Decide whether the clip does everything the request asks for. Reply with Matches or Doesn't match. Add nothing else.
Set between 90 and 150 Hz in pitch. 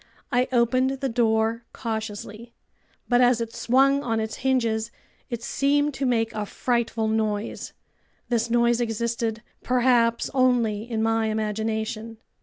Doesn't match